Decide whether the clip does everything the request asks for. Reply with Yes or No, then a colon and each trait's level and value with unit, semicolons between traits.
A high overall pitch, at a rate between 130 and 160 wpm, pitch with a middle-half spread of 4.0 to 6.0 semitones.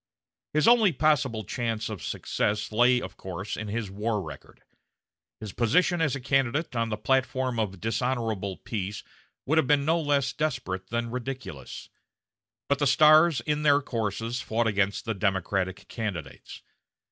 No: low, 115 Hz; average, 150 wpm; average, 5.1 semitones